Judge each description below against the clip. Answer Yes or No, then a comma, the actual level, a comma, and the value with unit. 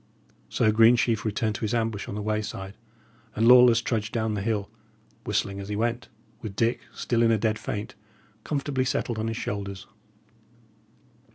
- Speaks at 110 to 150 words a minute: No, average, 165 wpm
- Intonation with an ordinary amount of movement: No, narrow, 2.0 semitones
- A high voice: No, low, 110 Hz